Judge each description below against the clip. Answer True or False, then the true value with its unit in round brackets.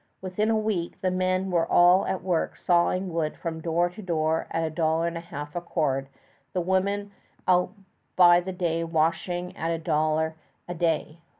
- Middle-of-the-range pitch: True (175 Hz)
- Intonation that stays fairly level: True (2.2 semitones)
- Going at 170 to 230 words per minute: True (185 wpm)